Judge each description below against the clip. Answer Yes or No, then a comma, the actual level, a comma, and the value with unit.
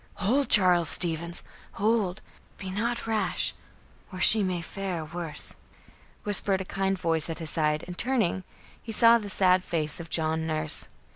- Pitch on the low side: No, medium, 185 Hz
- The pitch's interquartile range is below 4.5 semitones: Yes, average, 3.9 semitones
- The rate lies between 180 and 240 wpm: No, average, 155 wpm